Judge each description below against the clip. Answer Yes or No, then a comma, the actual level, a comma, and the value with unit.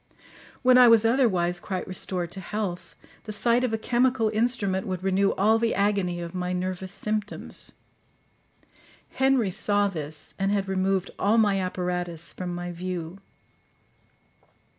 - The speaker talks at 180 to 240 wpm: No, average, 140 wpm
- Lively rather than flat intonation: No, average, 3.3 semitones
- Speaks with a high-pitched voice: Yes, high, 195 Hz